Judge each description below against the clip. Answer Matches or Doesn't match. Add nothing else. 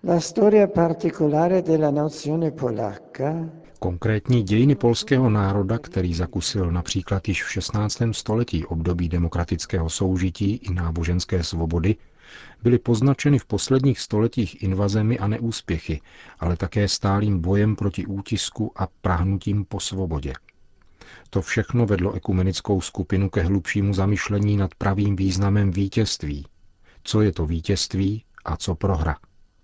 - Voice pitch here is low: Matches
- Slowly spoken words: Matches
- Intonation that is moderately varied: Matches